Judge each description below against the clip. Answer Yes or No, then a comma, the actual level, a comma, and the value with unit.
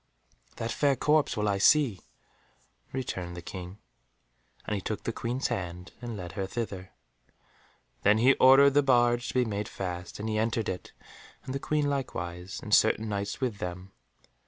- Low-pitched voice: Yes, low, 110 Hz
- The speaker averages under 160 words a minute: No, average, 170 wpm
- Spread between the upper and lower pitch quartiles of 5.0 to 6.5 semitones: Yes, average, 5.3 semitones